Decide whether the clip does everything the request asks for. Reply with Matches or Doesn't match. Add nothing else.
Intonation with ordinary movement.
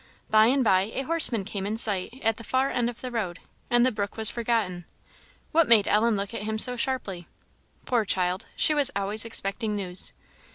Matches